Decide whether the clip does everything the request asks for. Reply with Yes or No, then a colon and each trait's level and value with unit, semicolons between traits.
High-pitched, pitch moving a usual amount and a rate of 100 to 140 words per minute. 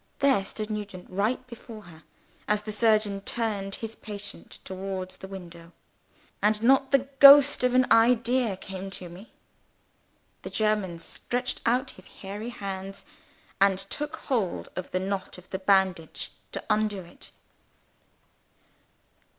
Yes: high, 205 Hz; average, 3.5 semitones; slow, 135 wpm